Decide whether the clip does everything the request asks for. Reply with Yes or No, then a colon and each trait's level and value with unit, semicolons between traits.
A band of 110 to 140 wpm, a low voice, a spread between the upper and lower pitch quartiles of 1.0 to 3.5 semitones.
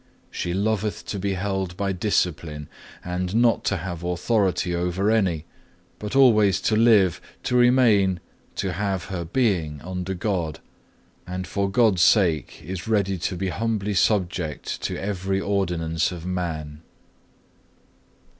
Yes: slow, 135 wpm; very low, 95 Hz; average, 2.8 semitones